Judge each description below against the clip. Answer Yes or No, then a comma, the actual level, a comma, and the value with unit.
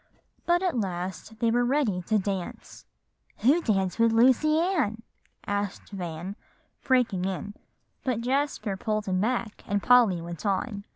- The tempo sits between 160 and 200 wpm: No, average, 140 wpm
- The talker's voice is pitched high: Yes, high, 215 Hz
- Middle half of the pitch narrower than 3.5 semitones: No, average, 4.5 semitones